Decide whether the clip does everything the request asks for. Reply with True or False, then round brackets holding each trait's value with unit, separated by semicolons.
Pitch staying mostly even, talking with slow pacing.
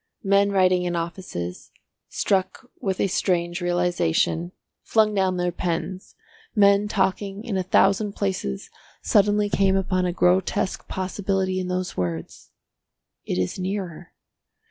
True (2.0 semitones; 125 wpm)